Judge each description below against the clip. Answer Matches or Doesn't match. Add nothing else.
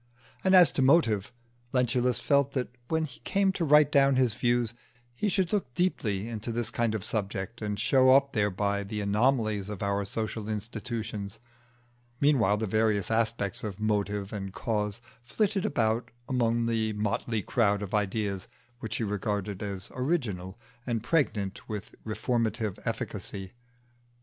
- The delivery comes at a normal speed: Matches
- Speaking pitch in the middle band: Doesn't match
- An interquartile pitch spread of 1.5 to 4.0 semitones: Matches